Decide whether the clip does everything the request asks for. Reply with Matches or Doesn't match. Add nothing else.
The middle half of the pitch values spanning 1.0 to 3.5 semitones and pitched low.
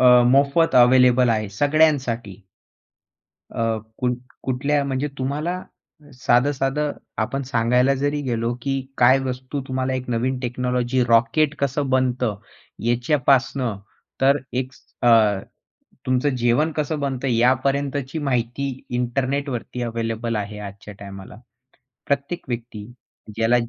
Matches